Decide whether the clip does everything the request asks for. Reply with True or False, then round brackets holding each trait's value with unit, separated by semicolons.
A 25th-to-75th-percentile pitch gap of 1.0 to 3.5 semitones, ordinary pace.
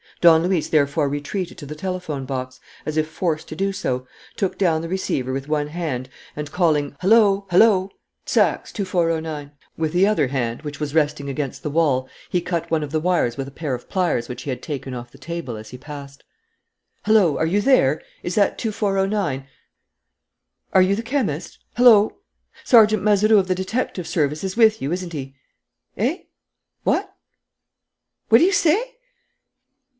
False (5.5 semitones; 175 wpm)